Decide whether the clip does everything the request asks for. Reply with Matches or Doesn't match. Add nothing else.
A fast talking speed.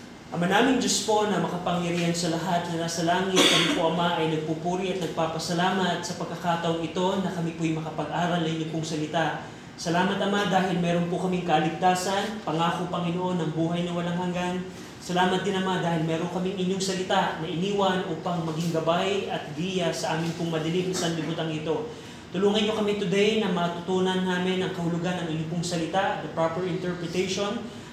Matches